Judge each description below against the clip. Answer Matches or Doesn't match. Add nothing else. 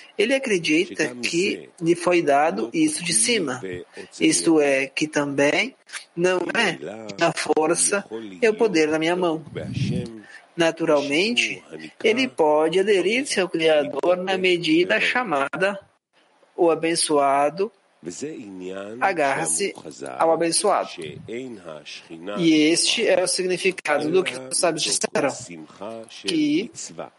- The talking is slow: Matches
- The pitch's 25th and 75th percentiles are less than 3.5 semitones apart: Doesn't match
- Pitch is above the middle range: Doesn't match